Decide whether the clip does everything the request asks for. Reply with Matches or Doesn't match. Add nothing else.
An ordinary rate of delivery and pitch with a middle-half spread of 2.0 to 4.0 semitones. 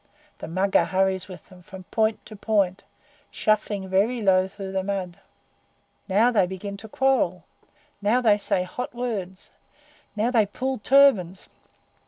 Matches